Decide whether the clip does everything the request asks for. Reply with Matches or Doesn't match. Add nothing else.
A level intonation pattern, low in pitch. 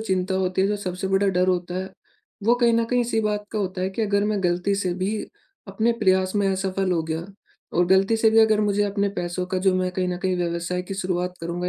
Doesn't match